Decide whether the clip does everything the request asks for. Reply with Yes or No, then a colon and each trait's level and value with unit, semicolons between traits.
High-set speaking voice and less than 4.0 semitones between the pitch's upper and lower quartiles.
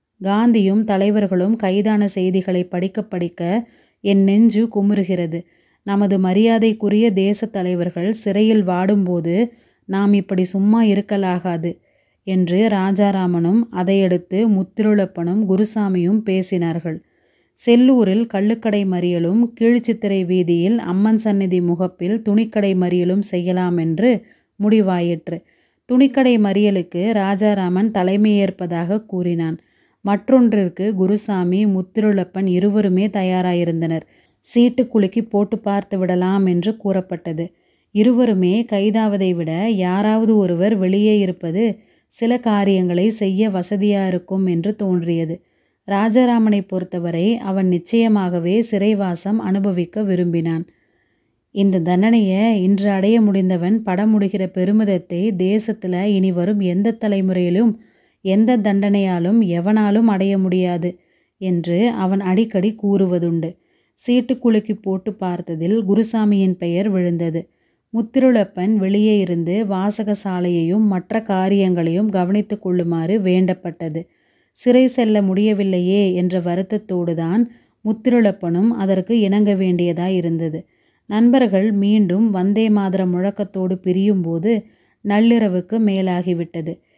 Yes: high, 195 Hz; average, 2.9 semitones